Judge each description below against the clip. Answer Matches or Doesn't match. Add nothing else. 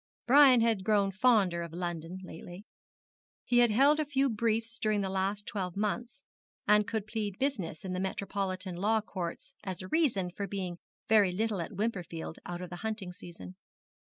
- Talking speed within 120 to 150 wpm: Doesn't match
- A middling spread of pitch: Matches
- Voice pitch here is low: Doesn't match